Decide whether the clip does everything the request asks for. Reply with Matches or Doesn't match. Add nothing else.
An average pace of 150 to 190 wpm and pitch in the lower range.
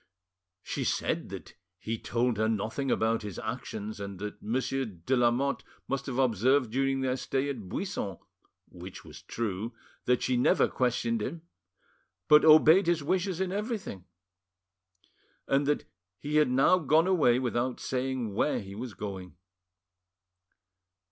Doesn't match